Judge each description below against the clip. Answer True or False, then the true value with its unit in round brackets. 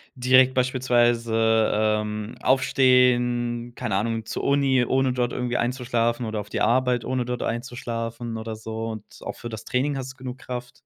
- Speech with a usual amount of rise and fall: False (2.0 semitones)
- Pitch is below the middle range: True (120 Hz)